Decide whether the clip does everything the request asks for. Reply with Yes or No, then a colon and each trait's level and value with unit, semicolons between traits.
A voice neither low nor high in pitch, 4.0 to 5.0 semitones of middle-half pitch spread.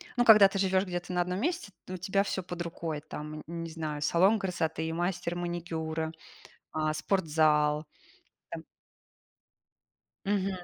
No: medium, 175 Hz; average, 3.1 semitones